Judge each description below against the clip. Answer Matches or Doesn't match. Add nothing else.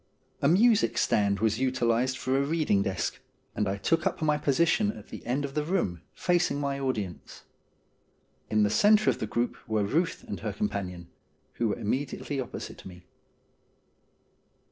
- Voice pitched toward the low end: Matches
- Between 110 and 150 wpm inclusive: Doesn't match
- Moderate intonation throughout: Doesn't match